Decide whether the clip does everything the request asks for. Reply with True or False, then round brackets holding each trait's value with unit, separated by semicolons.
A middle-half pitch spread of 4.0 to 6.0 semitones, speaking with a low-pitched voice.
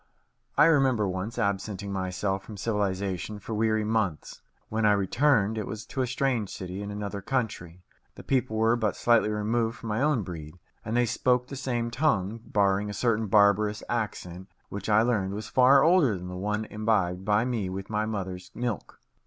False (3.1 semitones; 105 Hz)